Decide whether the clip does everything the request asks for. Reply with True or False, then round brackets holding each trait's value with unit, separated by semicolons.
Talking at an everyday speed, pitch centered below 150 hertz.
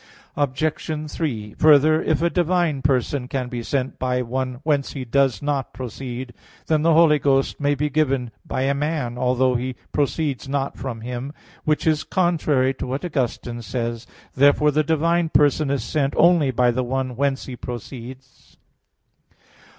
True (170 wpm; 135 Hz)